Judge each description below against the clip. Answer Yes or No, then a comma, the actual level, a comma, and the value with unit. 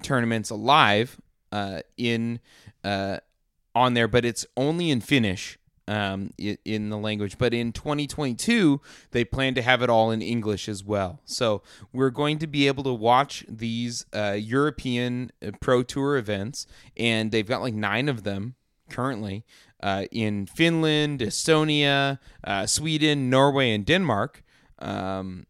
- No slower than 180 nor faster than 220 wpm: No, average, 145 wpm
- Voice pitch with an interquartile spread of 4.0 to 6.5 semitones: Yes, average, 4.8 semitones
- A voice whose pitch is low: Yes, low, 120 Hz